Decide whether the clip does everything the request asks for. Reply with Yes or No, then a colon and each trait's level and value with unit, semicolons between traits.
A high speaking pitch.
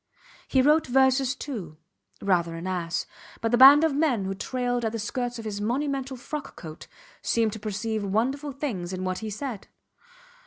Yes: high, 230 Hz